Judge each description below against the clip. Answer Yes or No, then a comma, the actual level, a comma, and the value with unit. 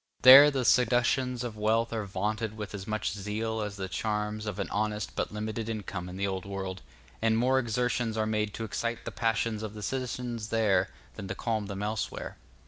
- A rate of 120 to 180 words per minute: No, average, 200 wpm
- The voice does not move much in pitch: Yes, narrow, 2.0 semitones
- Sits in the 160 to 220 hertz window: No, low, 110 Hz